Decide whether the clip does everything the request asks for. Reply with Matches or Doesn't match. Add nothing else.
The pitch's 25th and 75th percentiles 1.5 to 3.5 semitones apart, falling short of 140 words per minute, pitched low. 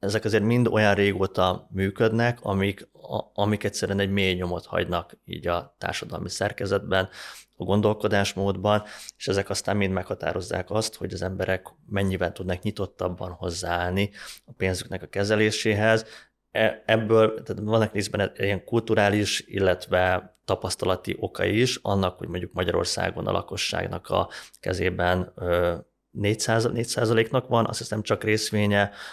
Matches